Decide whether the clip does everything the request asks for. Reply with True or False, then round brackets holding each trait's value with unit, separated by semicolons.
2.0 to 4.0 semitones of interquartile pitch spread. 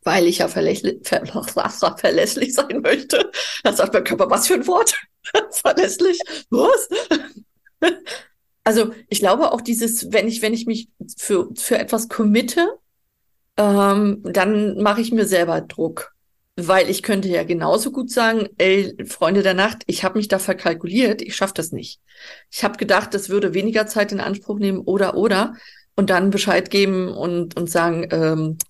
True (3.6 semitones)